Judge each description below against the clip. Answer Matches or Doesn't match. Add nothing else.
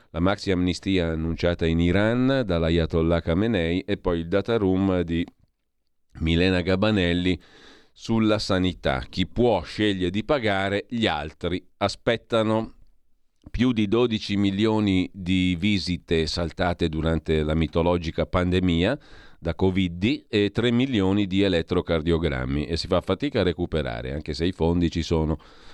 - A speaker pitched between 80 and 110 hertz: Matches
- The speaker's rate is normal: Matches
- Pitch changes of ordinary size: Matches